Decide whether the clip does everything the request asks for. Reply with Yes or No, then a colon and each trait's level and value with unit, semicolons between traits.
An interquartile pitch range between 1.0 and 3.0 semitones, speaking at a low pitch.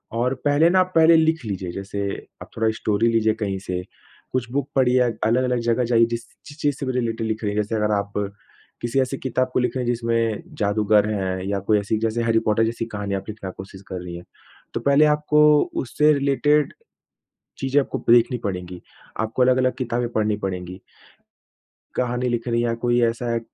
No: average, 3.7 semitones; low, 115 Hz